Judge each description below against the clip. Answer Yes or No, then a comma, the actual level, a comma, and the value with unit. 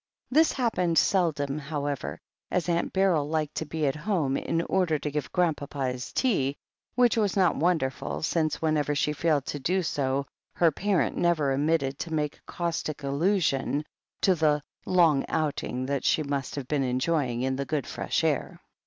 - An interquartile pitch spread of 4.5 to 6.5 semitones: No, average, 3.6 semitones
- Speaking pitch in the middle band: Yes, medium, 150 Hz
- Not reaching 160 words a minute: No, average, 175 wpm